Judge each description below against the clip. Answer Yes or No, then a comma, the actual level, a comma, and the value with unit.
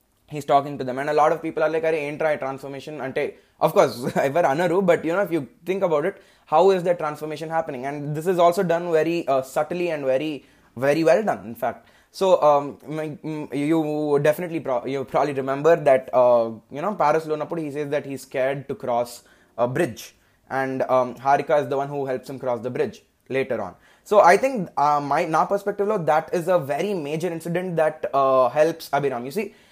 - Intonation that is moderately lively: Yes, average, 3.6 semitones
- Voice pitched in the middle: Yes, medium, 150 Hz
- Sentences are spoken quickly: Yes, fast, 210 wpm